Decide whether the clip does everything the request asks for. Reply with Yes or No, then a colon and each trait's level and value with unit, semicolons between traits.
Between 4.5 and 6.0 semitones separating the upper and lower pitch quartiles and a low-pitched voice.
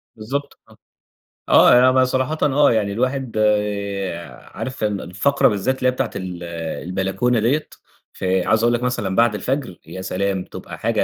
Yes: average, 5.0 semitones; low, 110 Hz